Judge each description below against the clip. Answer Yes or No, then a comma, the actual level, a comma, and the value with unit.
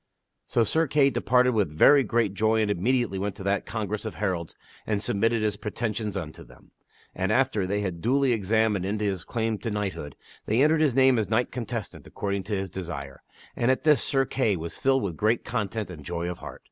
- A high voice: No, low, 105 Hz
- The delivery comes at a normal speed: No, fast, 210 wpm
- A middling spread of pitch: Yes, average, 3.7 semitones